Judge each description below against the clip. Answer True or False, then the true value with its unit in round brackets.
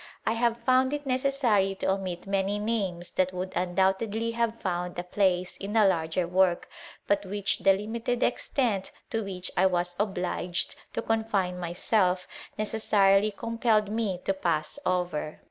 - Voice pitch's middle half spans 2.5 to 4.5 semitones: True (3.6 semitones)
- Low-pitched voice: False (195 Hz)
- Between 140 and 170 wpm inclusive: True (145 wpm)